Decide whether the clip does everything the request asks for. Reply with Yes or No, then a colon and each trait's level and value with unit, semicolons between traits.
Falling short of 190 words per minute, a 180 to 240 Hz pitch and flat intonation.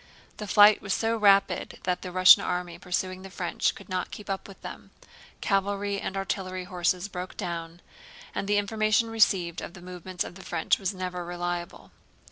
Yes: average, 180 wpm; medium, 185 Hz; narrow, 2.0 semitones